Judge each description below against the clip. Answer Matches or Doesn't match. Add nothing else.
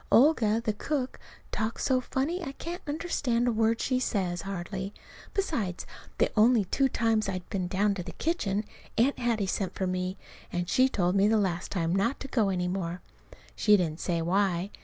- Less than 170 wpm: Doesn't match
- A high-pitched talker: Matches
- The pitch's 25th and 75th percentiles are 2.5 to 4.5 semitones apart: Doesn't match